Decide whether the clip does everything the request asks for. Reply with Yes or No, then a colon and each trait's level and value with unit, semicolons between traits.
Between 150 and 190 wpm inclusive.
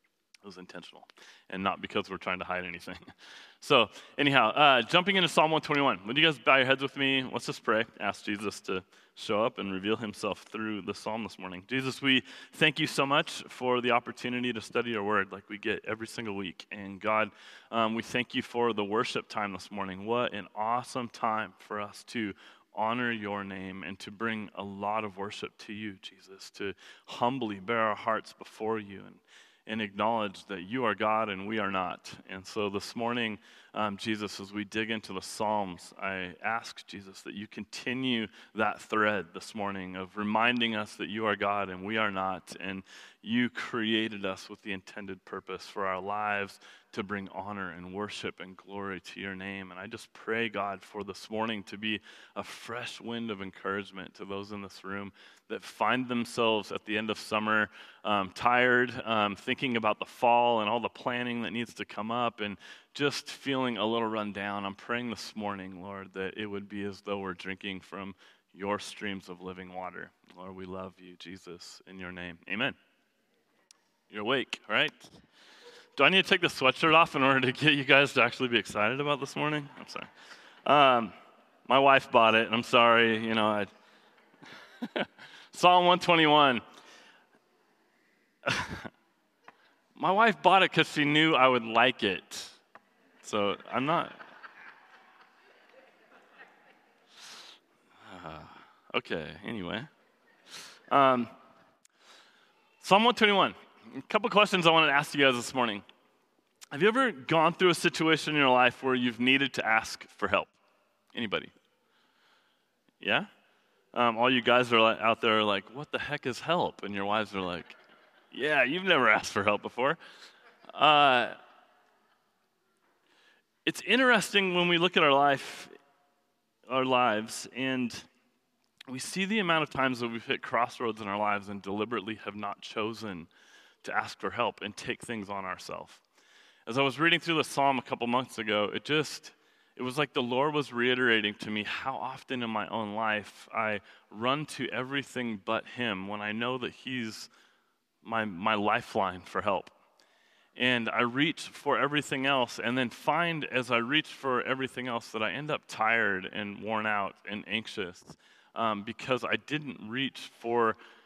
Yes: average, 175 wpm